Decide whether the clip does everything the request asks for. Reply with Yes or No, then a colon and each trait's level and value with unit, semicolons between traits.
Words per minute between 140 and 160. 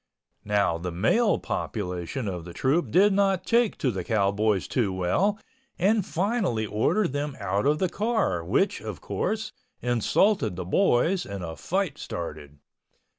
Yes: average, 150 wpm